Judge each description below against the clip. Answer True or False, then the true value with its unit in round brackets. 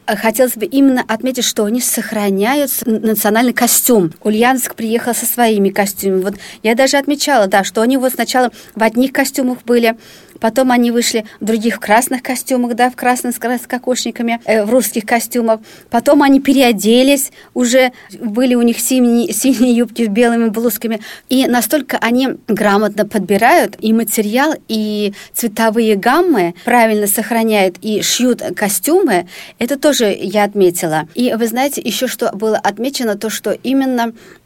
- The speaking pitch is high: True (235 Hz)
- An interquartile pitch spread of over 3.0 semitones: False (2.7 semitones)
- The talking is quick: False (150 wpm)